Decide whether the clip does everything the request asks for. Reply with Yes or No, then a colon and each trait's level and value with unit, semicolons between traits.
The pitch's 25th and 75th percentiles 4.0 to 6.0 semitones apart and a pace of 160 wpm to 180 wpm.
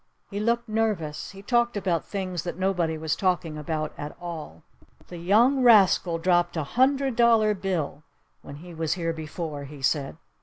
Yes: average, 5.1 semitones; average, 165 wpm